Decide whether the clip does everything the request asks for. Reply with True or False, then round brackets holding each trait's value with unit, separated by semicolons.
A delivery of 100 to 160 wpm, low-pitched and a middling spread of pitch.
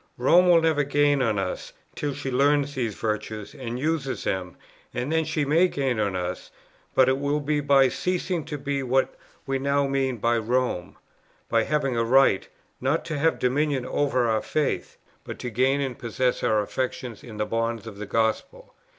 False (185 wpm; 130 Hz; 3.9 semitones)